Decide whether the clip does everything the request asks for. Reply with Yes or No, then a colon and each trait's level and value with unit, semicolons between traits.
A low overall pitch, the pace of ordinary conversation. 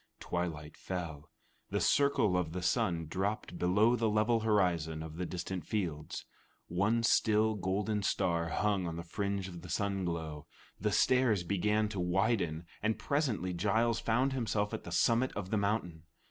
Yes: very low, 95 Hz; average, 160 wpm